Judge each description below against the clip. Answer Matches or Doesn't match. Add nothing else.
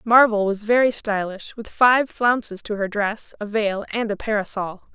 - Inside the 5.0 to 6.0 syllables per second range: Doesn't match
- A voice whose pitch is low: Doesn't match